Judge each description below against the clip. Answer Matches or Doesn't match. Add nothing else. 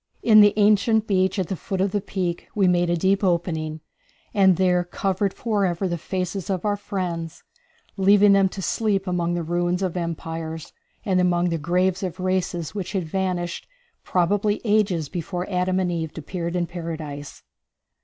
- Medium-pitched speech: Matches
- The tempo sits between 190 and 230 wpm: Doesn't match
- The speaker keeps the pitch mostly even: Matches